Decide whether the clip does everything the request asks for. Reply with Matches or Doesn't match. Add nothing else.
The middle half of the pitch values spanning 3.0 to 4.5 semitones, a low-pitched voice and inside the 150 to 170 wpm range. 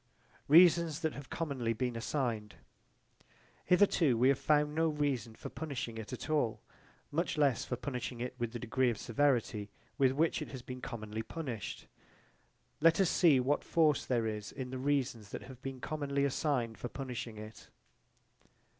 Matches